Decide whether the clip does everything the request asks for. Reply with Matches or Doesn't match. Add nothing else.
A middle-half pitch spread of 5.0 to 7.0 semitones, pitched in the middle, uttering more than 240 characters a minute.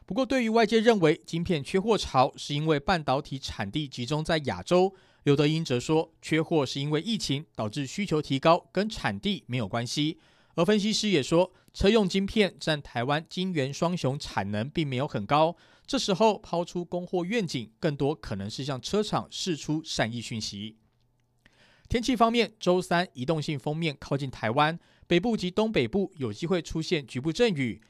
Matches